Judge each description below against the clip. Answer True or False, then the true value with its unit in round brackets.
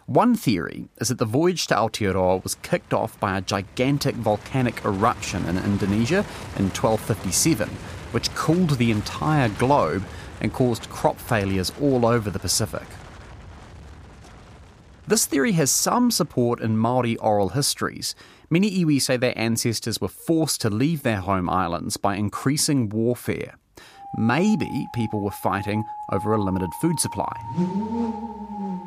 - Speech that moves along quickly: False (135 wpm)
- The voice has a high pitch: False (115 Hz)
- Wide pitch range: True (6.4 semitones)